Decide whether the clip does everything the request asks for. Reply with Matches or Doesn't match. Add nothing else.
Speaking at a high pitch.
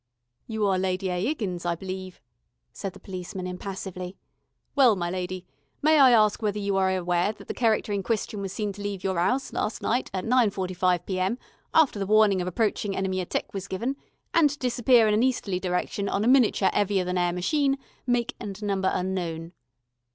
Matches